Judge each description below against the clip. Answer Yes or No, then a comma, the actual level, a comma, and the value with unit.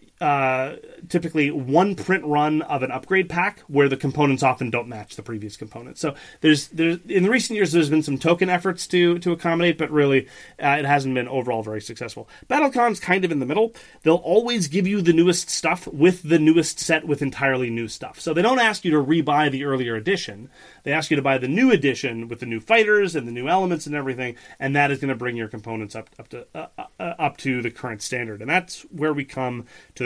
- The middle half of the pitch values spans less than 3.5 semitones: No, average, 5.2 semitones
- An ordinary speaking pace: No, fast, 230 wpm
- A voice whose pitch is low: No, medium, 150 Hz